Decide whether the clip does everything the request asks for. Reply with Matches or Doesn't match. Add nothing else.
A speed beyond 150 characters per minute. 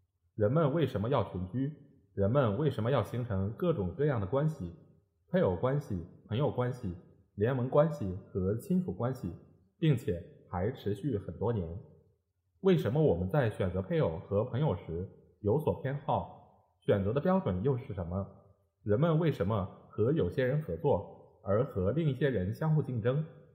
Matches